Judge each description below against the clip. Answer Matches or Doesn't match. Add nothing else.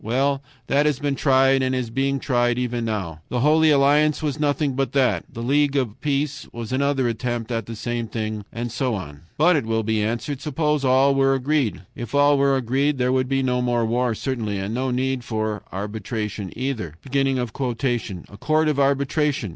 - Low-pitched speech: Matches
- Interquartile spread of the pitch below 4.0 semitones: Matches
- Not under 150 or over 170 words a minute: Doesn't match